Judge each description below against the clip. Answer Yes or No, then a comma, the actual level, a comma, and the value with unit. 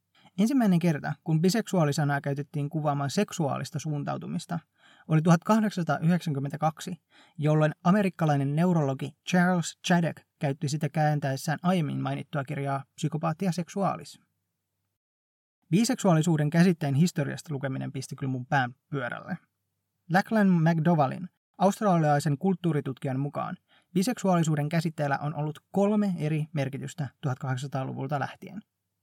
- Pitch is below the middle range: No, medium, 155 Hz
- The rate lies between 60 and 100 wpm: Yes, slow, 95 wpm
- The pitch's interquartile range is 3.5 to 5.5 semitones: Yes, average, 4.2 semitones